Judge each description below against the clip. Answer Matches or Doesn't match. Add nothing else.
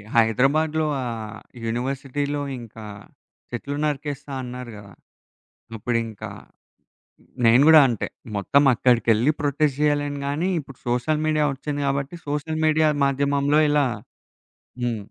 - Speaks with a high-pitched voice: Doesn't match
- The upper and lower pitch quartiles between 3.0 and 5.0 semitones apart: Matches